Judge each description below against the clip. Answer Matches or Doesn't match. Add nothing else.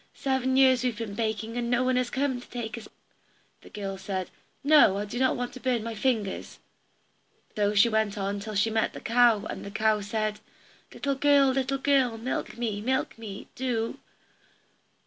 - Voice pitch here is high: Matches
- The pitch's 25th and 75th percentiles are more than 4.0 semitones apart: Doesn't match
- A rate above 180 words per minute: Matches